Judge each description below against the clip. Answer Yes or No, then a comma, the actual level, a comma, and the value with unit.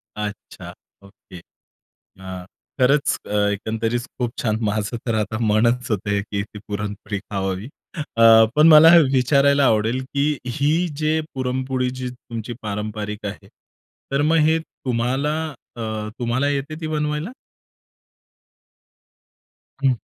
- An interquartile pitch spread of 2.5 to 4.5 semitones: No, average, 4.9 semitones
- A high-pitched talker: No, low, 120 Hz